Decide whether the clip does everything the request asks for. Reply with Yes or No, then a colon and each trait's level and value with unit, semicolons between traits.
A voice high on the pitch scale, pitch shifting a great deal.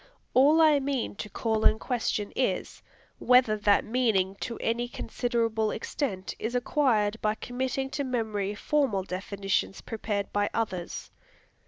No: high, 225 Hz; average, 3.6 semitones